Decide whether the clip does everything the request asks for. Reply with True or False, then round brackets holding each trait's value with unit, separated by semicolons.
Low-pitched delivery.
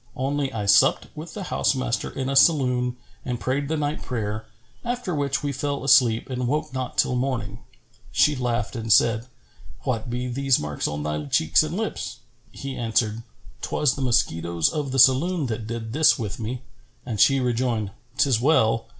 True (125 Hz)